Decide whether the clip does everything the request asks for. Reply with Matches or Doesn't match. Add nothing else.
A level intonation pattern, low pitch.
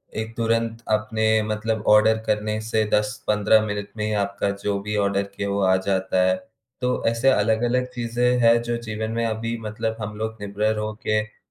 Matches